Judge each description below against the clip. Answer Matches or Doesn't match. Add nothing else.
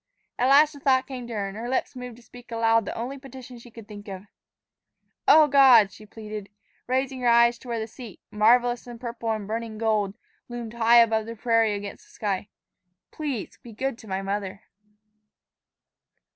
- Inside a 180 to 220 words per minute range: Matches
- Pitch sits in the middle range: Doesn't match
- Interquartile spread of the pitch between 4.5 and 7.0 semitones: Doesn't match